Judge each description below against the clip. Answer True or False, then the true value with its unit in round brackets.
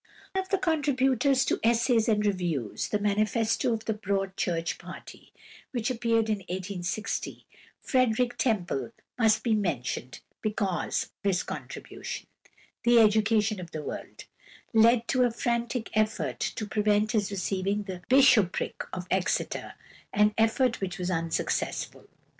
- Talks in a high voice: True (215 Hz)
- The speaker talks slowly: True (130 wpm)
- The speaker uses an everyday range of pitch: True (3.6 semitones)